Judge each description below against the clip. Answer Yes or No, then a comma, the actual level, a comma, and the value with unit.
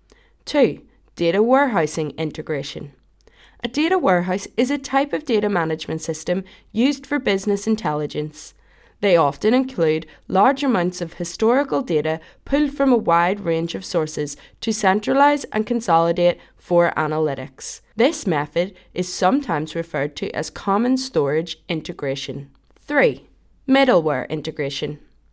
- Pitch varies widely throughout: Yes, wide, 7.3 semitones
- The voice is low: No, medium, 175 Hz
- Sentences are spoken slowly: Yes, slow, 125 wpm